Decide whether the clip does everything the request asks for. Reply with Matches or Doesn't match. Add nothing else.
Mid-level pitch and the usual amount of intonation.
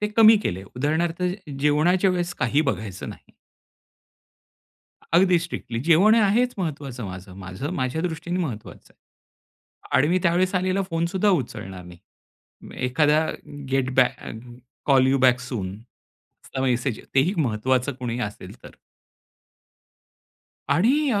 Doesn't match